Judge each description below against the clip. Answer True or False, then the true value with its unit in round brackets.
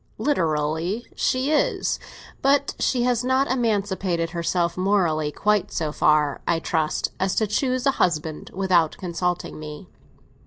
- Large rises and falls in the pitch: True (6.8 semitones)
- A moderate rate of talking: False (130 wpm)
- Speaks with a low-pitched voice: False (185 Hz)